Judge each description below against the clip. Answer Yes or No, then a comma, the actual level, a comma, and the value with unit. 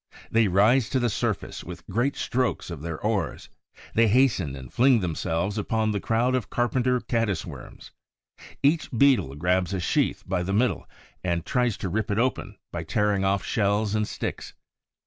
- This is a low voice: Yes, low, 105 Hz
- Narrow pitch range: No, average, 4.7 semitones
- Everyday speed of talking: Yes, average, 170 wpm